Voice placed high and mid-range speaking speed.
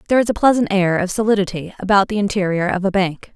No: high, 195 Hz; fast, 230 wpm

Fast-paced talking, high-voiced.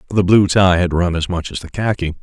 No: fast, 270 wpm; very low, 90 Hz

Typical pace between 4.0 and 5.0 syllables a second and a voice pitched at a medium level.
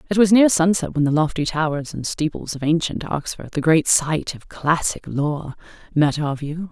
Yes: 4.7 syllables/s; medium, 160 Hz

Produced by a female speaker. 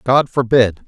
No: male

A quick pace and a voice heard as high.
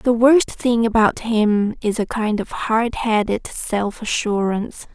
No: average, 160 wpm; high, 220 Hz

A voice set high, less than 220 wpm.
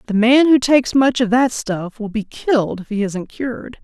No: high, 235 Hz; fast, 235 wpm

